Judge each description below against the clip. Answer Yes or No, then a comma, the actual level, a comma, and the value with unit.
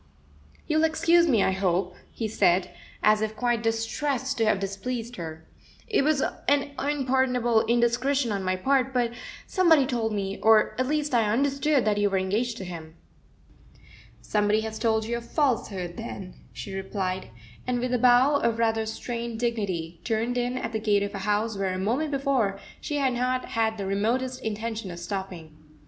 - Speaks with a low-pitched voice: No, high, 225 Hz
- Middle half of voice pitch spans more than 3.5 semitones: Yes, average, 4.2 semitones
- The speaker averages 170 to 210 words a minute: Yes, average, 175 wpm